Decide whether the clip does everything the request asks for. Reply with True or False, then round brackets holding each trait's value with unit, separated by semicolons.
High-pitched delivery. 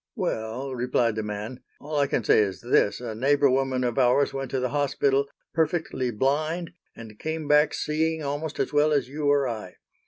False (135 Hz)